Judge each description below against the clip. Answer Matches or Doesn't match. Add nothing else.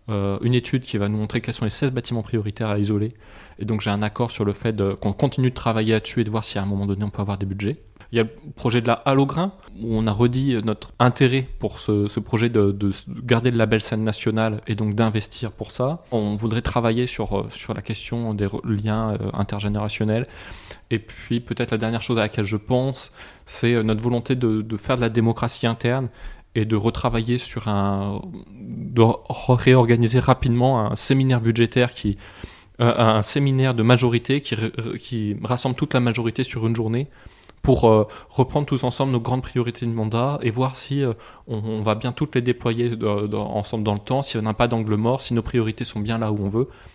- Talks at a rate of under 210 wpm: Doesn't match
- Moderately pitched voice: Doesn't match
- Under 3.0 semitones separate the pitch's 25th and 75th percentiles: Matches